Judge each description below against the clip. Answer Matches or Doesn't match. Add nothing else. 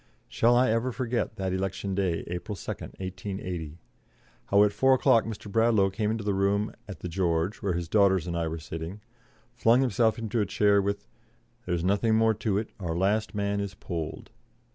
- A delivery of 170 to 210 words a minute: Matches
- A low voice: Matches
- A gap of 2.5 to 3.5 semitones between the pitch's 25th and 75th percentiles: Matches